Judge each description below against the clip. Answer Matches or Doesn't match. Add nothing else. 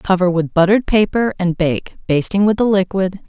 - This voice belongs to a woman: Matches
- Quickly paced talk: Doesn't match